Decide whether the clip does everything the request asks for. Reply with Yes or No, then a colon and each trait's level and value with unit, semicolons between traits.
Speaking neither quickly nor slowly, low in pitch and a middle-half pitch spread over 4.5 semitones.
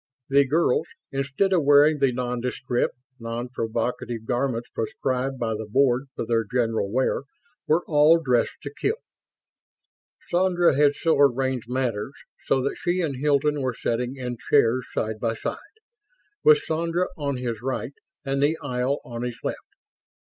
No: average, 150 wpm; low, 130 Hz; average, 3.2 semitones